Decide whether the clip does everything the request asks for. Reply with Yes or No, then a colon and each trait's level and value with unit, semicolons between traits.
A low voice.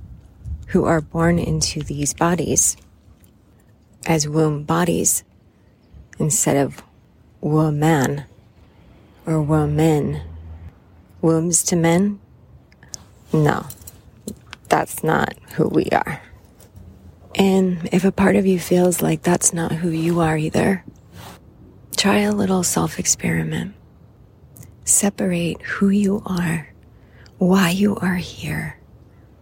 No: medium, 155 Hz